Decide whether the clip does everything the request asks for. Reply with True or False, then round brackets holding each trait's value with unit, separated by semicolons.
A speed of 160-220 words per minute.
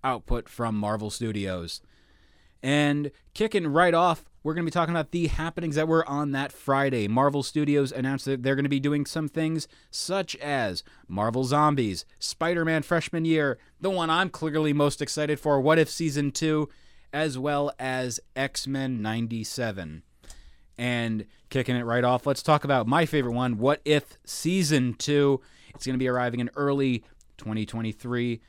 True (170 wpm)